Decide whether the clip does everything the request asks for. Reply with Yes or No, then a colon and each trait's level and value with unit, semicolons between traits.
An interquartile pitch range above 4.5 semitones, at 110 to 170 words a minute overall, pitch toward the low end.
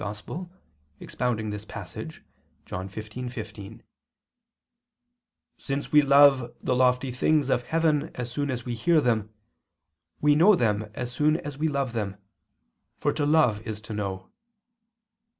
Yes: average, 5.0 semitones; average, 140 wpm; low, 125 Hz